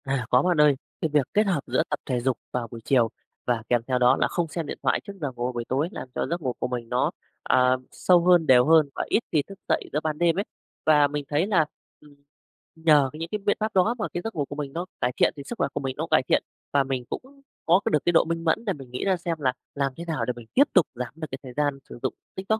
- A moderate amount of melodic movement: Yes, average, 4.9 semitones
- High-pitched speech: No, medium, 150 Hz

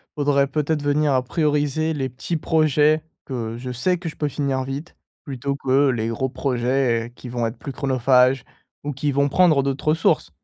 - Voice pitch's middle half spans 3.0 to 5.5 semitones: No, narrow, 2.6 semitones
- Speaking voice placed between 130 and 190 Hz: Yes, medium, 140 Hz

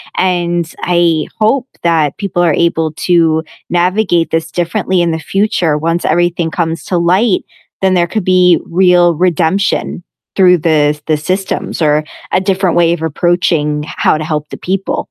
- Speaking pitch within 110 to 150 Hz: No, medium, 175 Hz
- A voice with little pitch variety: Yes, narrow, 2.1 semitones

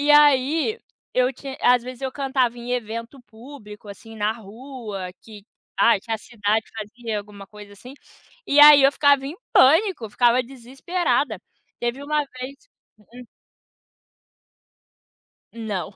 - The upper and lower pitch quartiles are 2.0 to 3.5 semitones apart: No, average, 4.0 semitones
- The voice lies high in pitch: Yes, high, 245 Hz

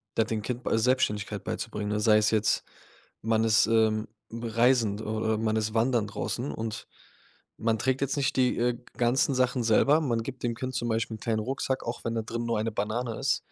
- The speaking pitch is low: Yes, low, 115 Hz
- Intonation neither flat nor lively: No, narrow, 2.2 semitones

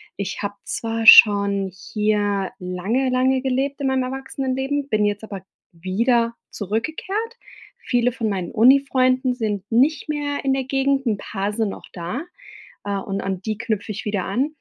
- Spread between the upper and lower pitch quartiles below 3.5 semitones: No, average, 4.7 semitones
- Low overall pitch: No, high, 230 Hz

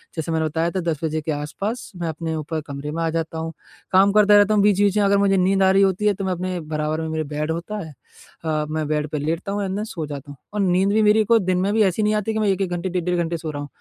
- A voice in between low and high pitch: Yes, medium, 175 Hz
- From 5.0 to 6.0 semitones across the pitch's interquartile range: No, average, 4.0 semitones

